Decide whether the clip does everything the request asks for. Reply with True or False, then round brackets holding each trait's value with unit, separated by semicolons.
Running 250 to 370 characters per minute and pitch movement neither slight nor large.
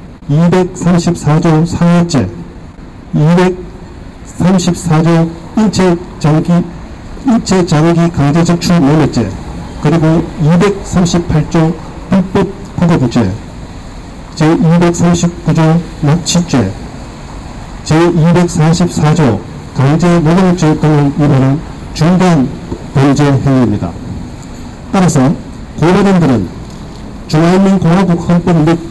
False (155 characters per minute; 3.5 semitones)